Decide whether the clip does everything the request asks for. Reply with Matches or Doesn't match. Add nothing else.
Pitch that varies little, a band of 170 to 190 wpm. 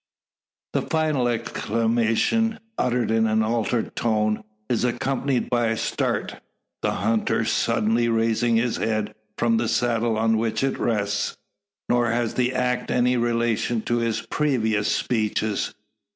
Doesn't match